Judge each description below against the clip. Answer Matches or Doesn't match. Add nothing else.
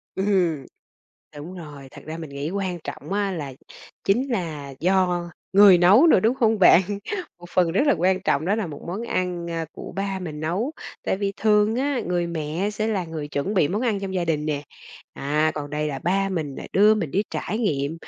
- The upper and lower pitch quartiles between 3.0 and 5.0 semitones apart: Matches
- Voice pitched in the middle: Matches